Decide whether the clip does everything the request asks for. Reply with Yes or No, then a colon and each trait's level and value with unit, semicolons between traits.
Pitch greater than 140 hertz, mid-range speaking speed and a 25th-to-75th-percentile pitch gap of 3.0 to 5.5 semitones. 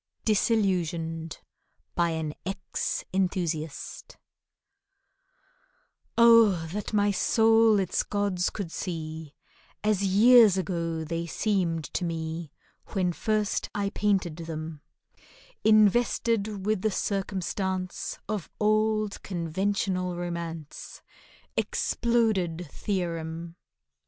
No: medium, 185 Hz; slow, 85 wpm; average, 4.0 semitones